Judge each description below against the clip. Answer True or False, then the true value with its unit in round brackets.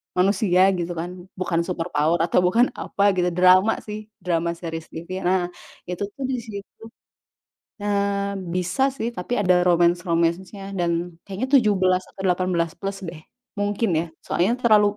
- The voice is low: False (185 Hz)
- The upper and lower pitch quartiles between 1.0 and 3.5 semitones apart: True (2.7 semitones)